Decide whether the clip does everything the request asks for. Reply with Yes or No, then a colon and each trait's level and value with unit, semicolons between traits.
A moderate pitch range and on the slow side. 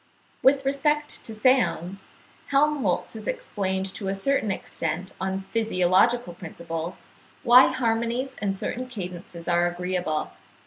No: wide, 6.1 semitones; slow, 120 wpm